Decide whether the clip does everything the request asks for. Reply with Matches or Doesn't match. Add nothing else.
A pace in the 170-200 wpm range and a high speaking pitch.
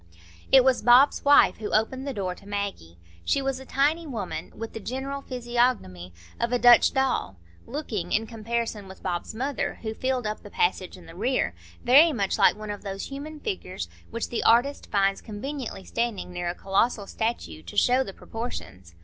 Matches